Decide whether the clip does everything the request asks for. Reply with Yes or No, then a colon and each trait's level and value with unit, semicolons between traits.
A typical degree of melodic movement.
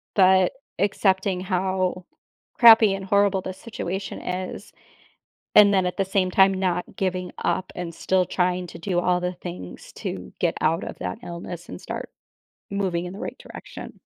No: narrow, 1.3 semitones